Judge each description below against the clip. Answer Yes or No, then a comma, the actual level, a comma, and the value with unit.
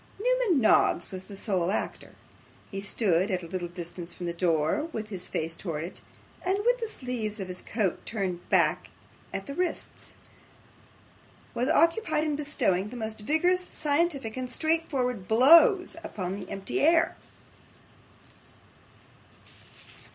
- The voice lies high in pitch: Yes, high, 220 Hz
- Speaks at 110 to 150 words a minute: Yes, average, 140 wpm